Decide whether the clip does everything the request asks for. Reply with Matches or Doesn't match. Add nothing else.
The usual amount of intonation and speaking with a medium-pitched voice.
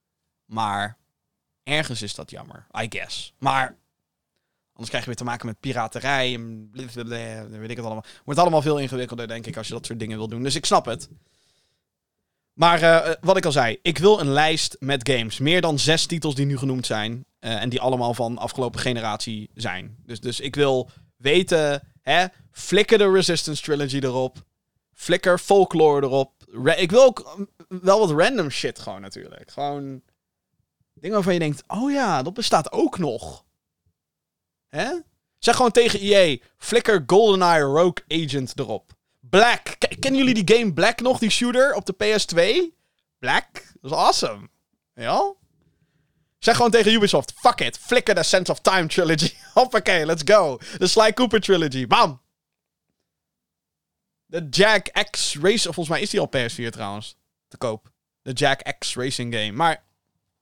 Doesn't match